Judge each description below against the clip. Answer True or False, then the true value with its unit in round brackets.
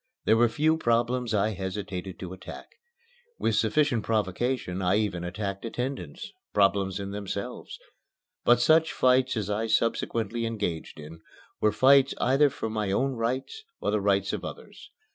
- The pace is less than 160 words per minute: True (150 wpm)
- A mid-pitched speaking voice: False (110 Hz)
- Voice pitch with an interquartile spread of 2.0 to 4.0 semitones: False (4.4 semitones)